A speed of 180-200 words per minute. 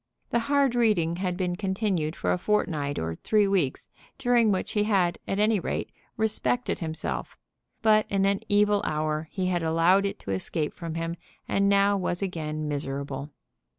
No: average, 170 wpm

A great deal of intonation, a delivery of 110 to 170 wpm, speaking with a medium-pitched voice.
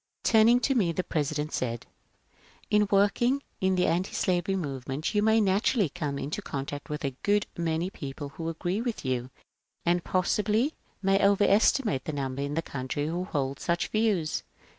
No: wide, 6.1 semitones; average, 180 wpm; medium, 175 Hz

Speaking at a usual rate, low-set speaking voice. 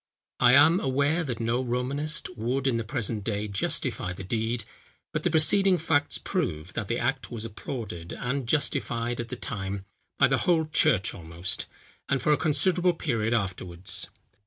Yes: average, 165 wpm; low, 120 Hz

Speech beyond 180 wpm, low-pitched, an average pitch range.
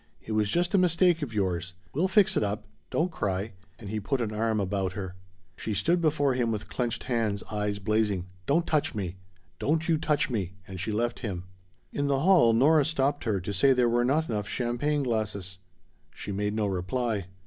No: average, 200 wpm; low, 115 Hz; wide, 6.0 semitones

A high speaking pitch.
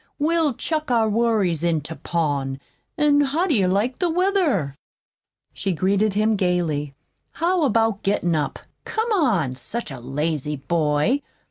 Yes: high, 200 Hz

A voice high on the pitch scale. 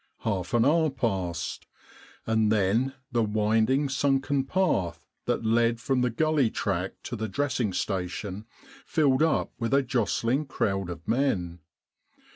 No: low, 115 Hz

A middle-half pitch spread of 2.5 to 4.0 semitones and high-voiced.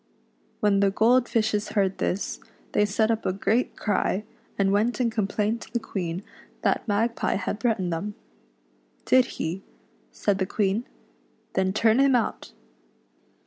Yes: average, 2.8 semitones; high, 210 Hz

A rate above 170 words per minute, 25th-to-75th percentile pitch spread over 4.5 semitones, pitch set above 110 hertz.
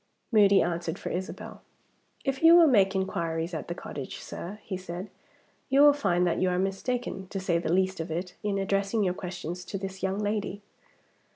No: average, 190 wpm; narrow, 2.5 semitones; high, 190 Hz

